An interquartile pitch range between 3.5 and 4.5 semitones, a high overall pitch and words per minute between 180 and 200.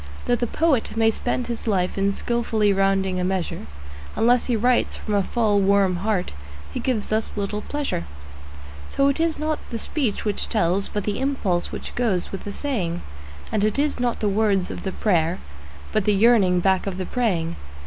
Yes: average, 3.8 semitones; high, 210 Hz; average, 190 wpm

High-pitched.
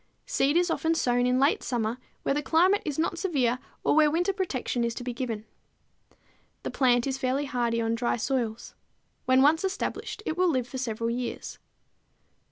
Yes: very high, 260 Hz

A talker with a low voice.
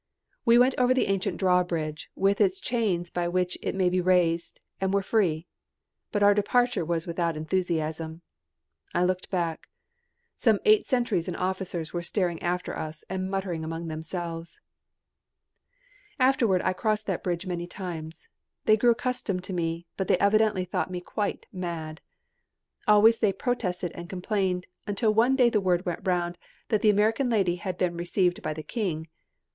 No: medium, 185 Hz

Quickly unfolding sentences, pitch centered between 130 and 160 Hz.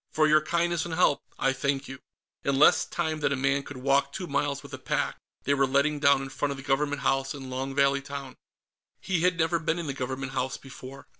Yes: fast, 235 wpm; medium, 140 Hz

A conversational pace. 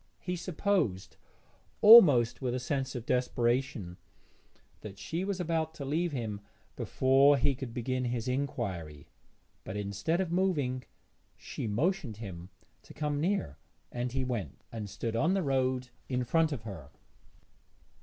Yes: average, 145 wpm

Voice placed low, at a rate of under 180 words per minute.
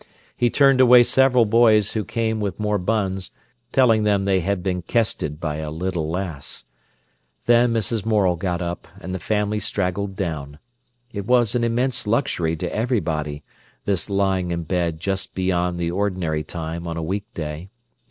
Yes: very low, 95 Hz; average, 160 wpm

